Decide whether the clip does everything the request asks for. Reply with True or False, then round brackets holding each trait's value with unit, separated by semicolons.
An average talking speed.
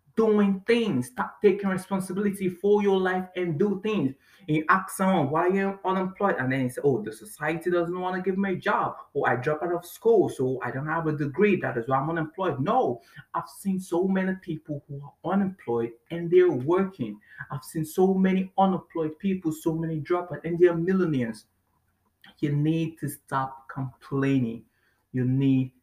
True (185 wpm)